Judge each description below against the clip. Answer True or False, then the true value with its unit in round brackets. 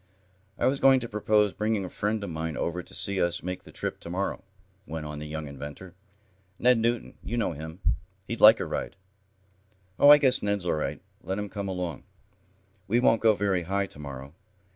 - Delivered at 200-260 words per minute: True (205 wpm)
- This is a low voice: True (100 Hz)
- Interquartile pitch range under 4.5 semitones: False (5.1 semitones)